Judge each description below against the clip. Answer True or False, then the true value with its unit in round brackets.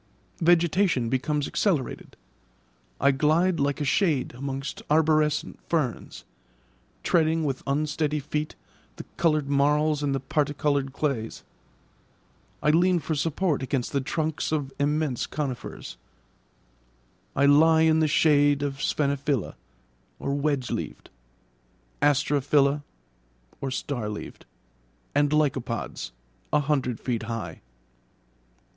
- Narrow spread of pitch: True (2.0 semitones)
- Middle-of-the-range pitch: True (145 Hz)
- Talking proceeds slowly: True (105 wpm)